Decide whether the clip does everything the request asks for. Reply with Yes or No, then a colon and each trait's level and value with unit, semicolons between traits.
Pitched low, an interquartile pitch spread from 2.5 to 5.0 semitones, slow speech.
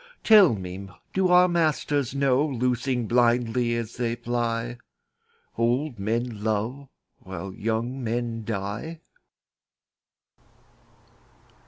Yes: low, 120 Hz; average, 3.2 semitones; slow, 95 wpm